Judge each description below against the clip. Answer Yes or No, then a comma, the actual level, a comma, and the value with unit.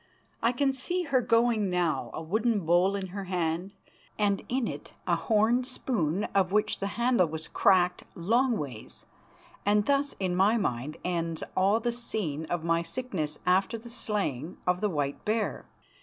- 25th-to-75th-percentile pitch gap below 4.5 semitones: No, wide, 5.4 semitones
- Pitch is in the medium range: No, high, 195 Hz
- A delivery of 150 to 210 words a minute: Yes, average, 165 wpm